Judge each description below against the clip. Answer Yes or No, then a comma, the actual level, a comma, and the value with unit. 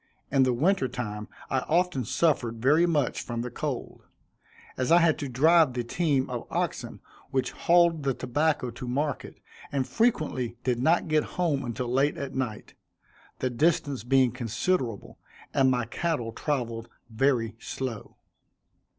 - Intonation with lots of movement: No, average, 4.2 semitones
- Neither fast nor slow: Yes, average, 150 wpm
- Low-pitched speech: Yes, low, 130 Hz